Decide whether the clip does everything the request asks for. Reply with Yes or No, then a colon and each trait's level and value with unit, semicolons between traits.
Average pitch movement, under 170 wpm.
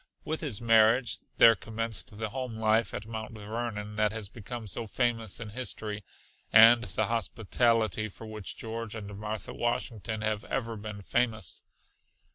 No: narrow, 1.5 semitones; average, 150 wpm